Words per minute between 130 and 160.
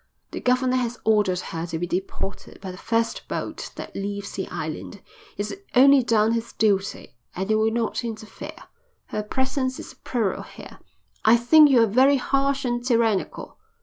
No: average, 170 wpm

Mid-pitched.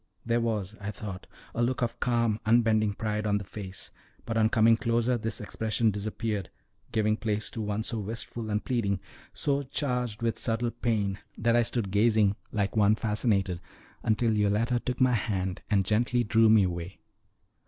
No: low, 110 Hz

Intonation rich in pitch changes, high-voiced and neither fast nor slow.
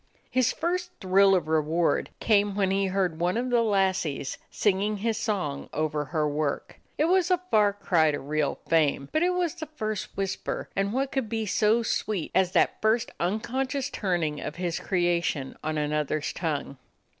Yes: wide, 6.2 semitones; high, 195 Hz; average, 175 wpm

